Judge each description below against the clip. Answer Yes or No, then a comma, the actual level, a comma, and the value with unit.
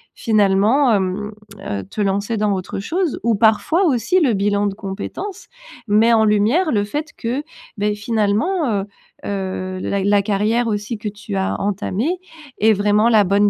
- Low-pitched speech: No, high, 210 Hz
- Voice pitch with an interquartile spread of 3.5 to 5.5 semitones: No, average, 2.7 semitones